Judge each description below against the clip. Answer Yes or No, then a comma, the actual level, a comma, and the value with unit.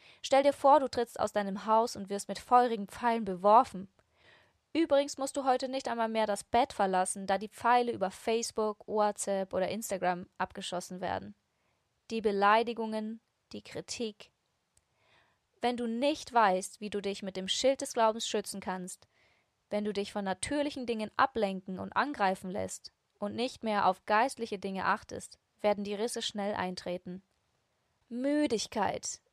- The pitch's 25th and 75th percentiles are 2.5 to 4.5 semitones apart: Yes, average, 3.5 semitones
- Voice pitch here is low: No, high, 210 Hz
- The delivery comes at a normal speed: Yes, average, 155 wpm